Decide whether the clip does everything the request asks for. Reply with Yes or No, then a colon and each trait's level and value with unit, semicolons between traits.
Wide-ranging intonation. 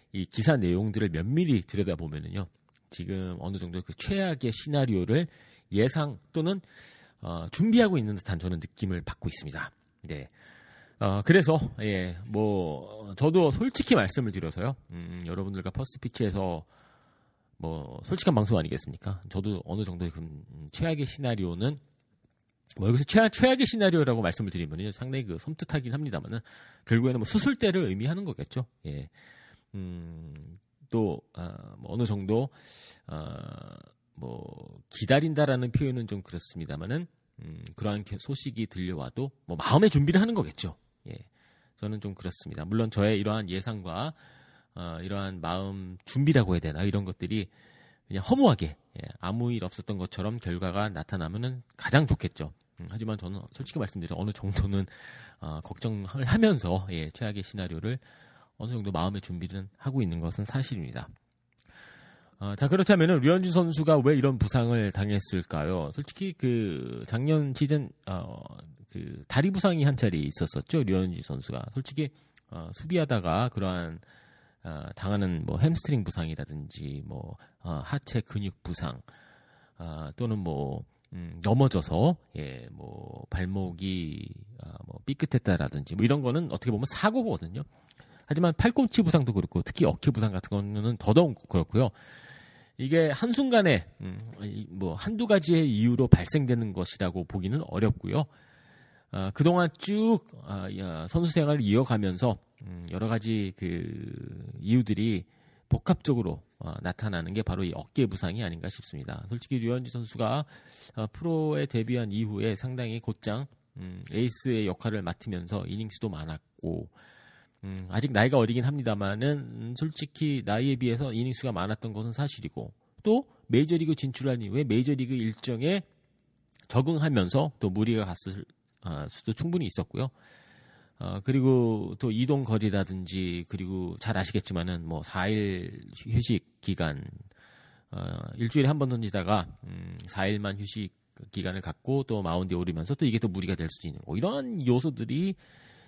Yes: wide, 6.6 semitones